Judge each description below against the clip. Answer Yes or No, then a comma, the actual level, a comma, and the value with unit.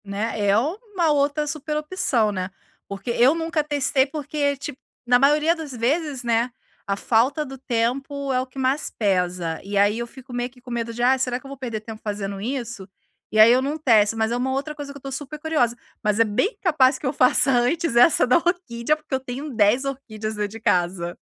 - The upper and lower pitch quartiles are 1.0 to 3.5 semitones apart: No, average, 4.4 semitones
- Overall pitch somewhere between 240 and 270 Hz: Yes, very high, 255 Hz